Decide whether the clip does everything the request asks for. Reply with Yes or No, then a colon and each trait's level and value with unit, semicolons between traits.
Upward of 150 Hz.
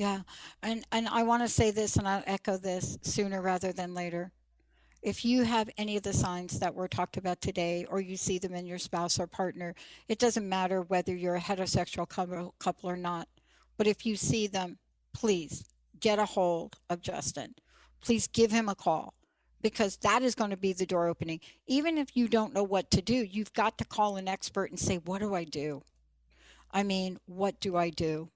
Yes: high, 190 Hz